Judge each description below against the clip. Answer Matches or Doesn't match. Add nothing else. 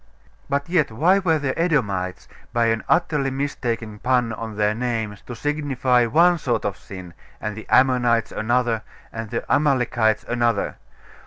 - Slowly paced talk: Doesn't match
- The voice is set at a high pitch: Doesn't match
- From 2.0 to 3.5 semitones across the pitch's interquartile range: Doesn't match